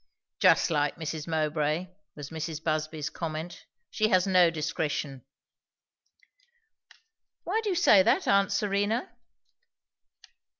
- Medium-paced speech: No, slow, 110 wpm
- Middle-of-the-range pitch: Yes, medium, 165 Hz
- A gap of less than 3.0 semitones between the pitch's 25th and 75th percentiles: No, average, 4.3 semitones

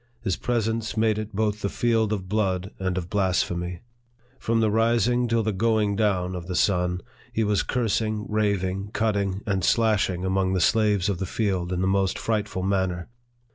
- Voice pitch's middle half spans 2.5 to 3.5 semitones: Yes, average, 2.9 semitones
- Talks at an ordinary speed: Yes, average, 175 wpm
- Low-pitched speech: Yes, low, 100 Hz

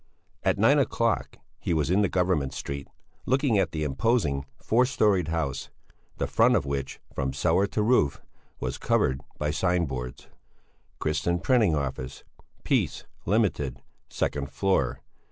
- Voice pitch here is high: No, very low, 80 Hz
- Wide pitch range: Yes, wide, 6.3 semitones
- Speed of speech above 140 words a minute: No, slow, 135 wpm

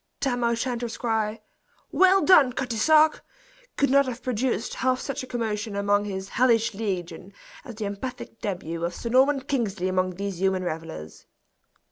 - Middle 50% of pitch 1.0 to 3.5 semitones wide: No, average, 4.8 semitones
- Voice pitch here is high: Yes, high, 225 Hz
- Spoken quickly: No, average, 155 wpm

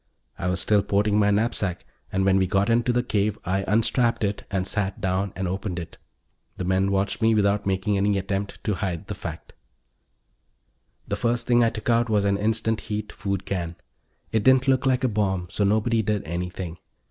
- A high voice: No, low, 100 Hz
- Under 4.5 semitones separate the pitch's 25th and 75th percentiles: Yes, narrow, 2.6 semitones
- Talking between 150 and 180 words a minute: No, average, 195 wpm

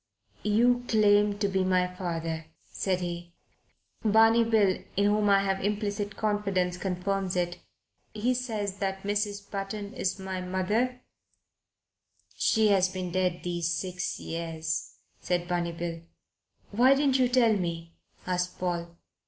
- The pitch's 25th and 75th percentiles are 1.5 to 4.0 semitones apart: Yes, average, 2.7 semitones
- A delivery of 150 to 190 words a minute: No, slow, 135 wpm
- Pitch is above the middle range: Yes, high, 195 Hz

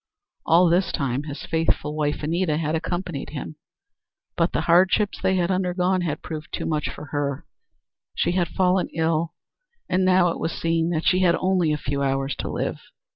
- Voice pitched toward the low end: No, medium, 165 Hz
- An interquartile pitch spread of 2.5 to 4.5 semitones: Yes, average, 3.2 semitones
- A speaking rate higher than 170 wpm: Yes, average, 180 wpm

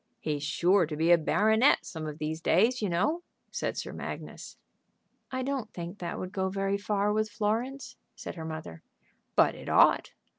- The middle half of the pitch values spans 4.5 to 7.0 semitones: Yes, average, 5.0 semitones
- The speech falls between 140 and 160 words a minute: No, average, 180 wpm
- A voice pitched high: Yes, high, 195 Hz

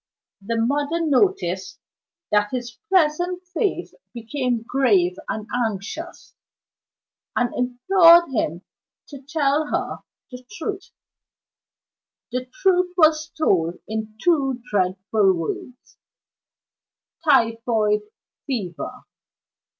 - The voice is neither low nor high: No, very high, 255 Hz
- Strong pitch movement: Yes, wide, 6.6 semitones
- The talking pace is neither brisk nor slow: No, slow, 90 wpm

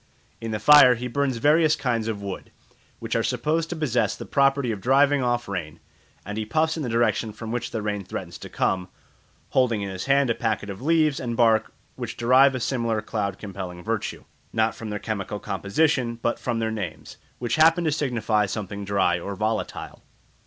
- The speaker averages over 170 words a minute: Yes, average, 195 wpm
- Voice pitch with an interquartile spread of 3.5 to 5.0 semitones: Yes, average, 4.4 semitones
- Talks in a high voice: No, low, 115 Hz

